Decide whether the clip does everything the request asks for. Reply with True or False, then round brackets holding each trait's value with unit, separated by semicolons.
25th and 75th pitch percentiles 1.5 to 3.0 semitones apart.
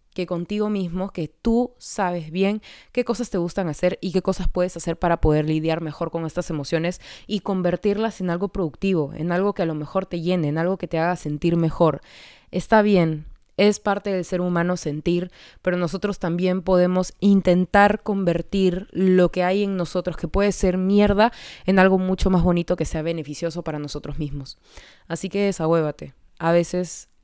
True (2.5 semitones)